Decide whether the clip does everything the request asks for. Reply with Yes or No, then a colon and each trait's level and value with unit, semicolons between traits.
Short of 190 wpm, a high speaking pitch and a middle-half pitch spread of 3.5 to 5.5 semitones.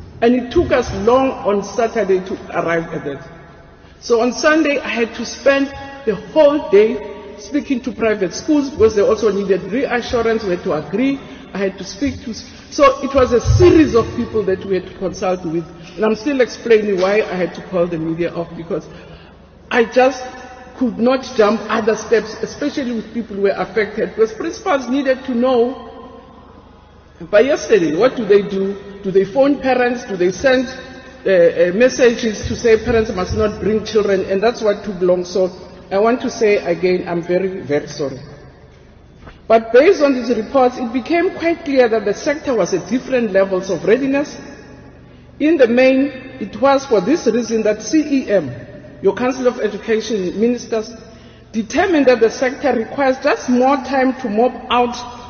Yes: average, 180 wpm; high, 230 Hz; average, 4.7 semitones